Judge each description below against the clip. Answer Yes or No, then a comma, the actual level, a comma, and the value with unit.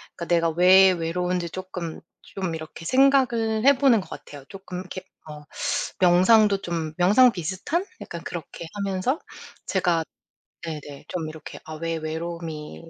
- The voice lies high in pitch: No, medium, 180 Hz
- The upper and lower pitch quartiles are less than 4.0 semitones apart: Yes, average, 3.2 semitones